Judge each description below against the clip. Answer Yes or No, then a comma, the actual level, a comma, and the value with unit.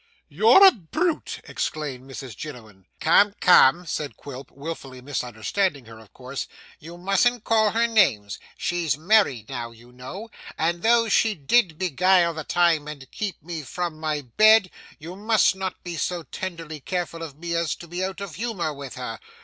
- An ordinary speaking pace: Yes, average, 170 wpm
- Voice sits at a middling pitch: Yes, medium, 165 Hz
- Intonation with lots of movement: Yes, wide, 5.7 semitones